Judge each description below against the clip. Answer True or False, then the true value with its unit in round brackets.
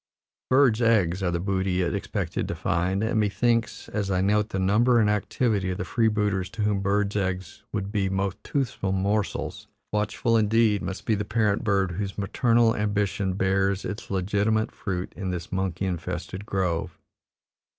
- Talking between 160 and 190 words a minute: True (170 wpm)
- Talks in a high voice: False (100 Hz)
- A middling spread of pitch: False (2.2 semitones)